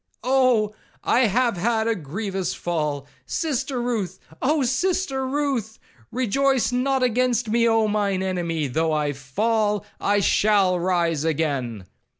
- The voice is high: Yes, high, 215 Hz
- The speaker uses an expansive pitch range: Yes, wide, 6.8 semitones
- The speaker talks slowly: Yes, slow, 115 wpm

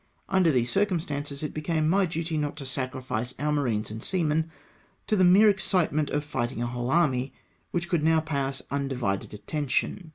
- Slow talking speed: No, average, 175 wpm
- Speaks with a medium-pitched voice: Yes, medium, 150 Hz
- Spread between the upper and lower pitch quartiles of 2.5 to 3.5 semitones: No, average, 4.2 semitones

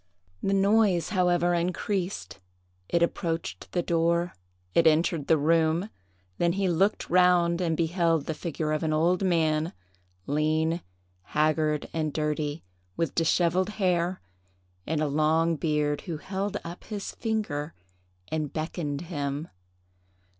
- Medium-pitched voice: Yes, medium, 165 Hz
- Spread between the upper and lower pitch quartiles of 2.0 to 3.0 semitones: Yes, narrow, 2.4 semitones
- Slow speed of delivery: Yes, slow, 125 wpm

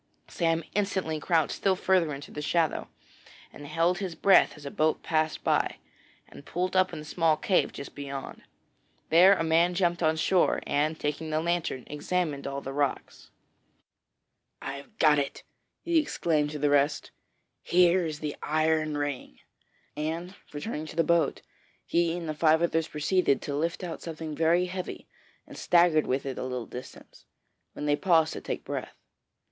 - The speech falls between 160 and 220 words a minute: Yes, average, 170 wpm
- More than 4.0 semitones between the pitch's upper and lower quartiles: No, average, 2.8 semitones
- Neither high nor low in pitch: Yes, medium, 160 Hz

